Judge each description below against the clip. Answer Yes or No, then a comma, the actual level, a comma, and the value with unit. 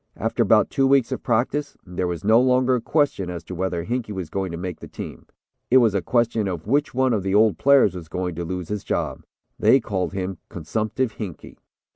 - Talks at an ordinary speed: No, fast, 220 wpm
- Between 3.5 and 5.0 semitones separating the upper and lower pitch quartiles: No, wide, 5.6 semitones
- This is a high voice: No, low, 100 Hz